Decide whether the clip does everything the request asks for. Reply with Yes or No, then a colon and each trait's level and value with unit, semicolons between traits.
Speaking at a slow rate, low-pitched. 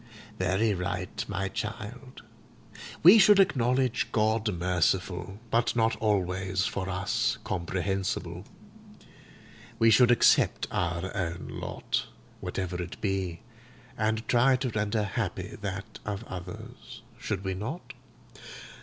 Yes: slow, 110 wpm; low, 100 Hz